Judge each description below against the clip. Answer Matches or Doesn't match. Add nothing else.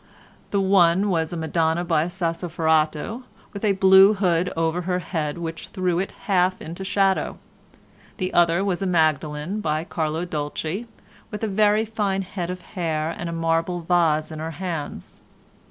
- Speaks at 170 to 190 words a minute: Doesn't match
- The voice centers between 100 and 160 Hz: Doesn't match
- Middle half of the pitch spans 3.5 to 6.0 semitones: Doesn't match